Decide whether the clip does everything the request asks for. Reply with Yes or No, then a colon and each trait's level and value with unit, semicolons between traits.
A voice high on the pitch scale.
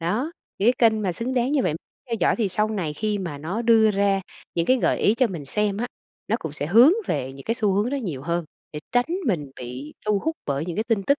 Yes: high, 205 Hz